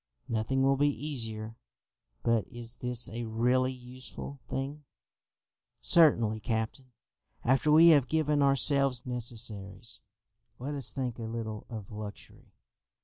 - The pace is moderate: No, slow, 120 wpm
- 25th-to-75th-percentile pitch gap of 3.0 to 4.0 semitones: Yes, average, 3.5 semitones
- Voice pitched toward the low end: Yes, low, 125 Hz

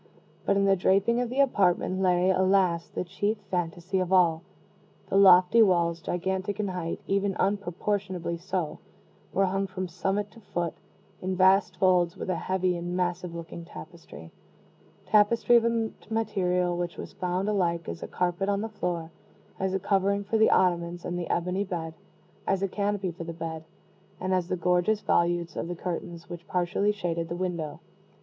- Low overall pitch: No, medium, 185 Hz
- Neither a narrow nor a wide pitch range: No, narrow, 2.3 semitones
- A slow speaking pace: No, average, 175 wpm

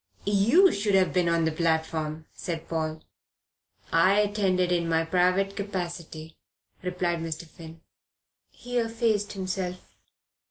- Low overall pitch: No, medium, 180 Hz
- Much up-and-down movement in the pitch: No, average, 3.3 semitones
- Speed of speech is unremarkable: No, slow, 120 wpm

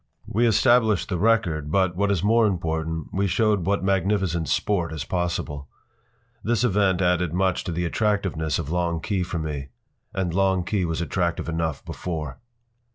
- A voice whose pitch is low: Yes, very low, 90 Hz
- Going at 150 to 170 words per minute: Yes, average, 160 wpm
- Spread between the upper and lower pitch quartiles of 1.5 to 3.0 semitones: No, average, 3.5 semitones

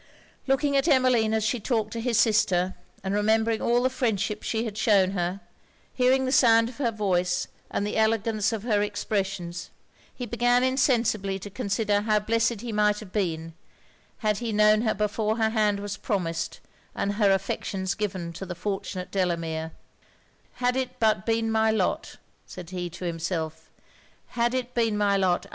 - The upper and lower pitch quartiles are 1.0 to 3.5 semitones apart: Yes, average, 3.0 semitones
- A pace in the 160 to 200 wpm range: Yes, average, 170 wpm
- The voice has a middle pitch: No, high, 210 Hz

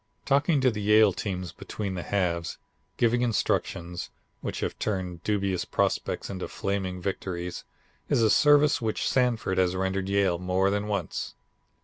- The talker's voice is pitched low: Yes, low, 100 Hz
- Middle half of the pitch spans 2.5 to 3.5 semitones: Yes, average, 3.1 semitones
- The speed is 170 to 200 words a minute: No, average, 145 wpm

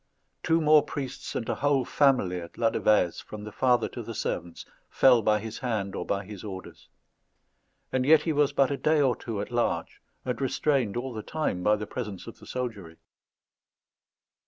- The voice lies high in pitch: No, low, 120 Hz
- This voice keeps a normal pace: Yes, average, 185 wpm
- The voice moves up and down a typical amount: Yes, average, 4.6 semitones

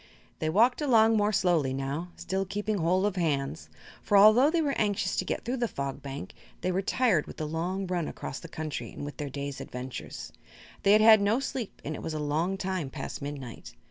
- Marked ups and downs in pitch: Yes, wide, 6.2 semitones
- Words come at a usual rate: No, fast, 215 wpm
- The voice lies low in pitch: No, medium, 185 Hz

